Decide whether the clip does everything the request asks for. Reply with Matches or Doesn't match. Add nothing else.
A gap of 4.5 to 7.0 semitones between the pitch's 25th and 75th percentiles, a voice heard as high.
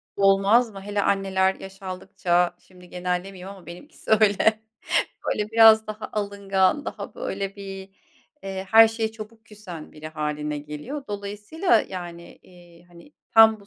Doesn't match